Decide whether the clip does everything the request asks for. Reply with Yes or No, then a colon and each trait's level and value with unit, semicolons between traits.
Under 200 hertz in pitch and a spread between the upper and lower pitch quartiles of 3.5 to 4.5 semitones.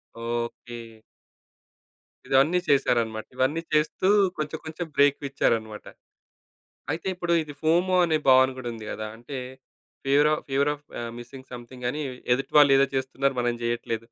Yes: low, 135 Hz; average, 3.8 semitones